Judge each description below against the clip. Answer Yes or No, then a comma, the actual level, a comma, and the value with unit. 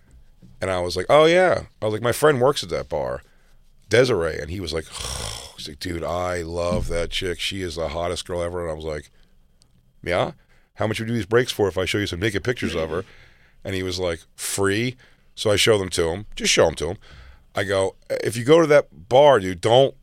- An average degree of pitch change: No, wide, 5.9 semitones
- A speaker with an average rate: No, fast, 250 wpm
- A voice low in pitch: Yes, very low, 95 Hz